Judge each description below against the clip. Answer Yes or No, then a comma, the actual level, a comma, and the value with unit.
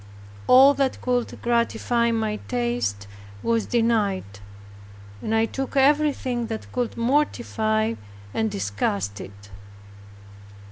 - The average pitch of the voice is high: Yes, high, 230 Hz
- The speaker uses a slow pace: Yes, slow, 100 wpm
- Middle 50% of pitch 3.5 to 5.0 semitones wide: No, average, 2.7 semitones